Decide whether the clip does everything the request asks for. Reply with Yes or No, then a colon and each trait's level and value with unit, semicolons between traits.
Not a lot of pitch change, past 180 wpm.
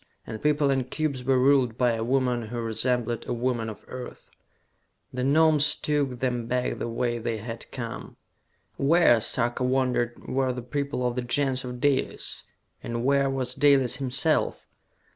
No: narrow, 2.3 semitones; average, 160 wpm